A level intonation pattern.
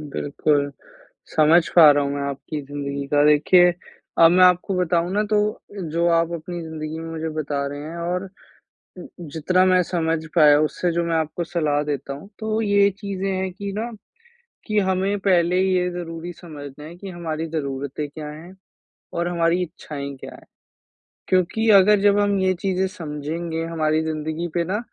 No: average, 3.4 semitones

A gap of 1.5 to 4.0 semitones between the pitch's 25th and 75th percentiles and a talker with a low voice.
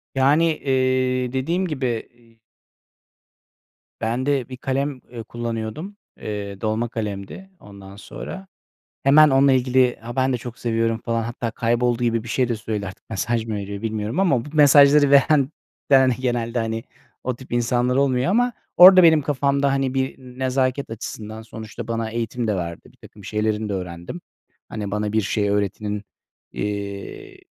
Yes: average, 3.5 semitones; low, 120 Hz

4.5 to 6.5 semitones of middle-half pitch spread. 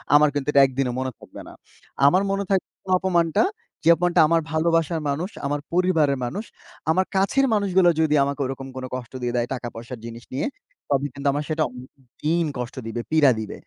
Yes: average, 4.8 semitones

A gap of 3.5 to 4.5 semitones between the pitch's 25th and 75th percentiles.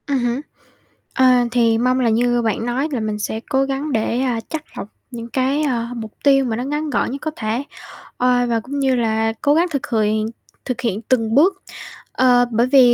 No: average, 3.0 semitones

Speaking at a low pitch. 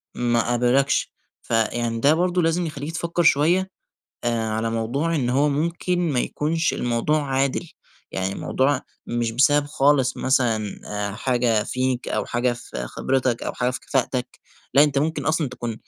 Yes: low, 130 Hz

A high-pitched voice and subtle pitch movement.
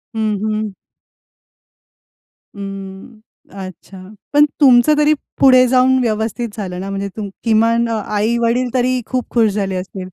No: high, 220 Hz; average, 3.9 semitones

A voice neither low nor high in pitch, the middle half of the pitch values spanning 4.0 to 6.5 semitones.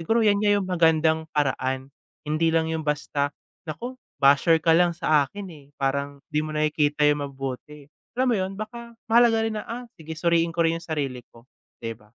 Yes: medium, 160 Hz; average, 4.5 semitones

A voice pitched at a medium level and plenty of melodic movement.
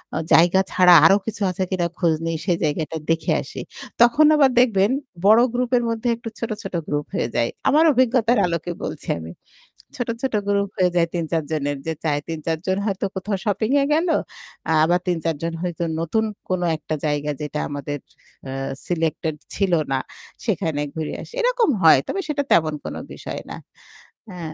Yes: medium, 175 Hz; wide, 5.7 semitones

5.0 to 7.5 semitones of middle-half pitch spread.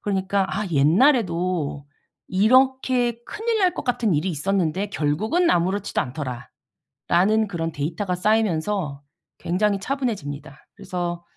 Yes: wide, 5.4 semitones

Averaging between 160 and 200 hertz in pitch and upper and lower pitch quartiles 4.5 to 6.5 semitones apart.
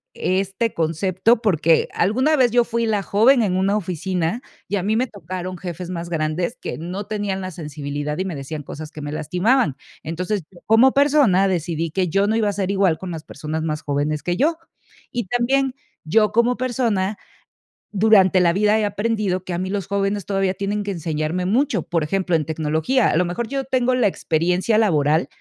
Yes: high, 190 Hz; average, 4.8 semitones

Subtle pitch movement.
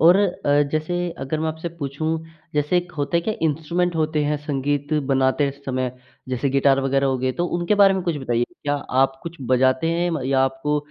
No: average, 3.7 semitones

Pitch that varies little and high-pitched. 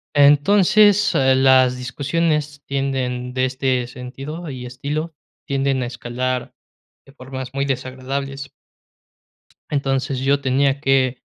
No: narrow, 1.6 semitones; low, 135 Hz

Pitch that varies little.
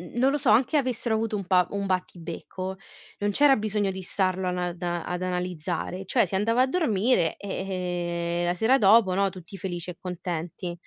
No: average, 3.2 semitones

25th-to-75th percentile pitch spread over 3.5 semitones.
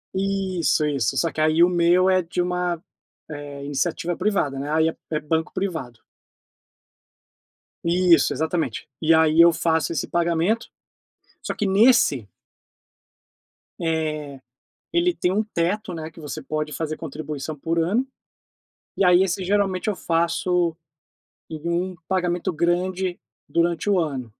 No: average, 2.8 semitones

